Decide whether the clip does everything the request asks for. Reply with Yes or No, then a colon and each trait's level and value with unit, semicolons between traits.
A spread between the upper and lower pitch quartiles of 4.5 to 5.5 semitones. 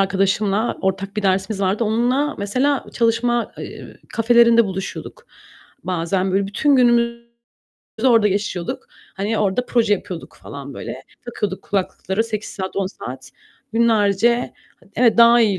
No: average, 3.5 semitones